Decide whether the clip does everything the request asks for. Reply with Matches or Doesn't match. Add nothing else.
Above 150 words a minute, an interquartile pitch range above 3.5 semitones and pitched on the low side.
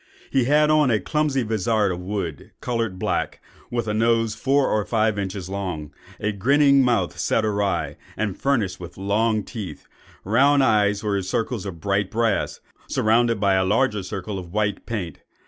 Doesn't match